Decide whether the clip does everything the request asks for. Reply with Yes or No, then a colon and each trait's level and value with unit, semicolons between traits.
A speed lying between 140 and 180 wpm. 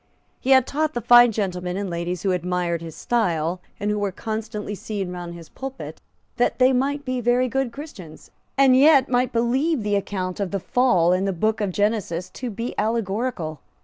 No: average, 190 wpm